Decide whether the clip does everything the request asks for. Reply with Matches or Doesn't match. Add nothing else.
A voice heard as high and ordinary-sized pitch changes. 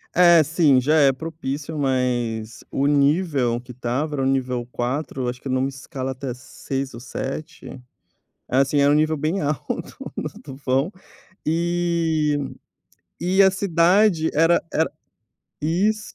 Doesn't match